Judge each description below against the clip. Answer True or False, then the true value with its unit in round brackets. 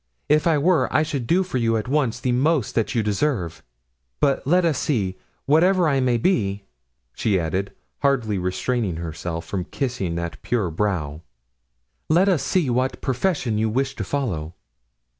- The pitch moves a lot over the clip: True (7.2 semitones)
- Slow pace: False (165 wpm)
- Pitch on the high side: False (120 Hz)